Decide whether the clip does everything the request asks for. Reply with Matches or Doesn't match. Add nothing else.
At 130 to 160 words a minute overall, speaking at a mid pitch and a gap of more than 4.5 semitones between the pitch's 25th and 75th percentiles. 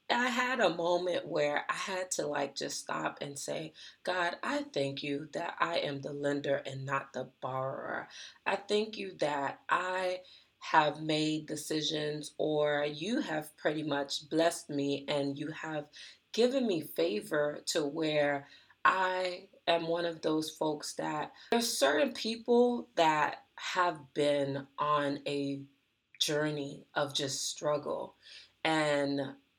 Doesn't match